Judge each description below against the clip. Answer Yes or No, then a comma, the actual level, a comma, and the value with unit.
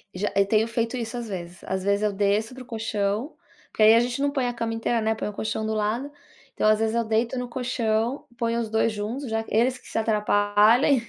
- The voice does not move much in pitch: Yes, narrow, 2.2 semitones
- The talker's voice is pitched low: No, high, 225 Hz